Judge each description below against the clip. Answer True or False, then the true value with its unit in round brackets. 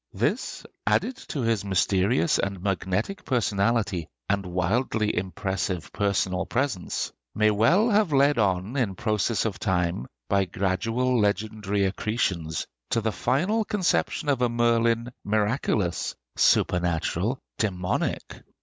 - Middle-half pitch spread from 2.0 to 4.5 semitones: True (4.2 semitones)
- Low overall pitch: True (105 Hz)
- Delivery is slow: True (115 wpm)